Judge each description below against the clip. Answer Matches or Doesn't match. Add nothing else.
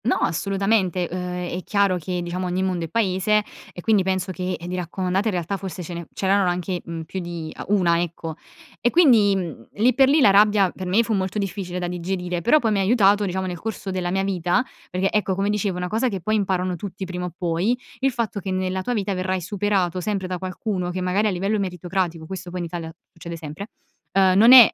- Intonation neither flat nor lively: Doesn't match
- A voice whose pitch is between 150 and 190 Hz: Matches